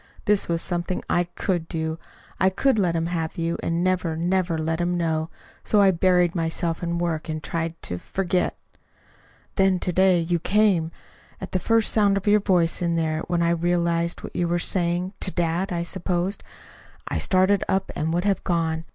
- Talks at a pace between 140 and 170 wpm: No, average, 190 wpm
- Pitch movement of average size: No, narrow, 2.1 semitones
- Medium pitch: Yes, medium, 175 Hz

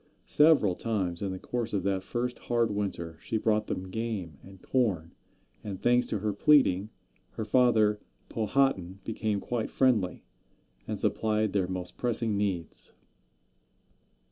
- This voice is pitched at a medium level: No, low, 105 Hz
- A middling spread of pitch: Yes, average, 3.8 semitones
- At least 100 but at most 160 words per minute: Yes, average, 140 wpm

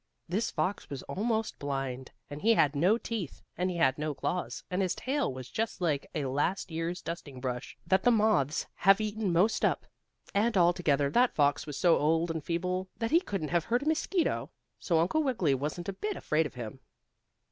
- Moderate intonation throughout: No, wide, 6.6 semitones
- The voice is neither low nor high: Yes, medium, 175 Hz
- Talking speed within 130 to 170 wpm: No, average, 200 wpm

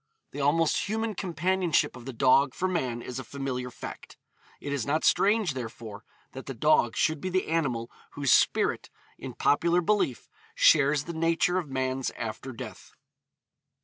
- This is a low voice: No, medium, 145 Hz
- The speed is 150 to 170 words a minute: Yes, average, 160 wpm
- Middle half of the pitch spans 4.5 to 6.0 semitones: Yes, average, 4.8 semitones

